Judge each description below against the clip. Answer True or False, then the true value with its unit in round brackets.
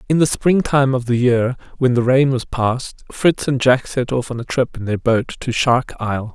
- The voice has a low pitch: True (125 Hz)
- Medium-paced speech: False (245 wpm)